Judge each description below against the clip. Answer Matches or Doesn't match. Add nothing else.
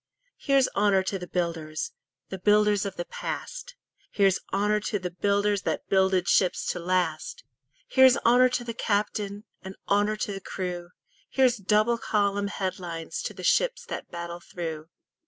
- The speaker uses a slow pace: Doesn't match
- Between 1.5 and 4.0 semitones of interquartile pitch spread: Matches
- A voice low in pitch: Doesn't match